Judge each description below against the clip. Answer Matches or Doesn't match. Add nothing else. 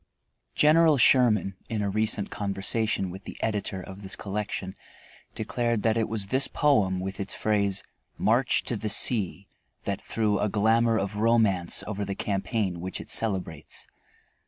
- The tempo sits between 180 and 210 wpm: Doesn't match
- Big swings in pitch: Doesn't match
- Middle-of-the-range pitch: Doesn't match